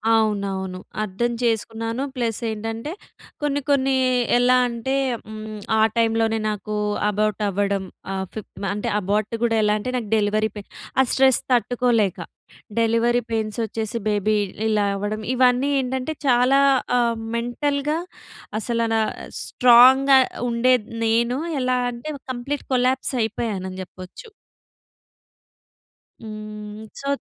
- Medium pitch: No, high, 230 Hz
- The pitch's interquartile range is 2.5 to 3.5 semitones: Yes, average, 3.0 semitones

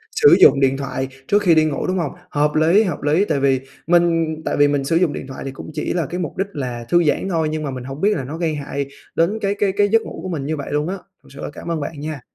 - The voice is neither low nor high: Yes, medium, 155 Hz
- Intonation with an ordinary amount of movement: Yes, average, 3.9 semitones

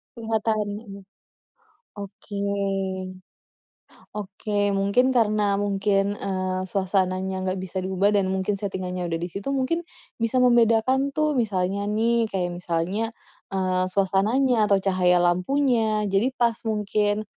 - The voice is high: Yes, high, 200 Hz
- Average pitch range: Yes, average, 3.0 semitones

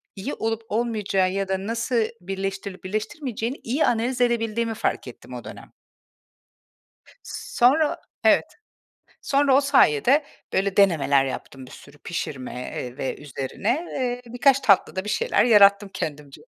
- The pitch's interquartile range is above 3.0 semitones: Yes, average, 4.8 semitones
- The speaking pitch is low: No, high, 210 Hz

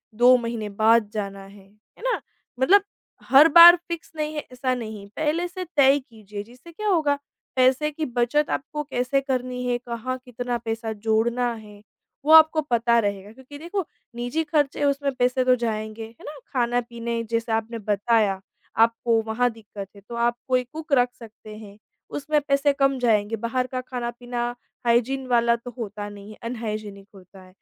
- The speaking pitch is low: No, high, 240 Hz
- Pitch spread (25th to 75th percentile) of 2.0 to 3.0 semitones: No, average, 3.7 semitones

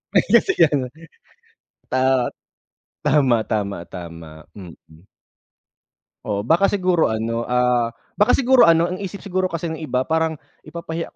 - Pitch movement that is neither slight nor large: No, wide, 6.6 semitones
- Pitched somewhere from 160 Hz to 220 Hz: No, medium, 145 Hz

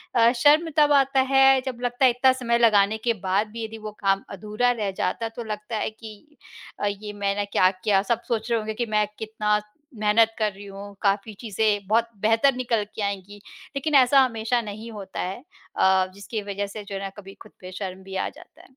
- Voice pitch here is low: No, high, 215 Hz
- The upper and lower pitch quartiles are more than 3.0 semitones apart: No, average, 2.7 semitones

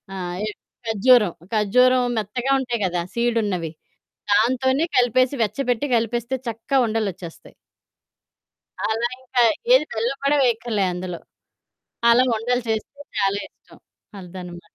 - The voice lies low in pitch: No, high, 230 Hz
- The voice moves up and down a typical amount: Yes, average, 3.9 semitones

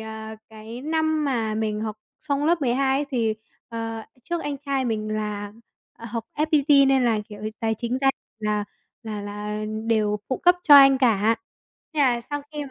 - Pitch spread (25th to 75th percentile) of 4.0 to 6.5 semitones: Yes, average, 4.4 semitones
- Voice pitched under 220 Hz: No, high, 235 Hz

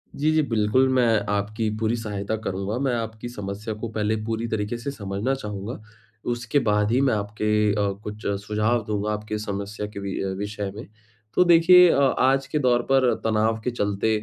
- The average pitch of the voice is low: Yes, low, 110 Hz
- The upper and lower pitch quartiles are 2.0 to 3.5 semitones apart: Yes, average, 2.8 semitones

